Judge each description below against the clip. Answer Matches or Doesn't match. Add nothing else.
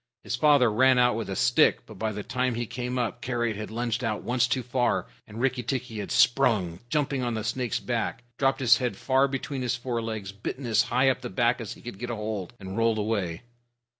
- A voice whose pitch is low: Matches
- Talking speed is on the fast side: Matches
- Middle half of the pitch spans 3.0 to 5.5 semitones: Doesn't match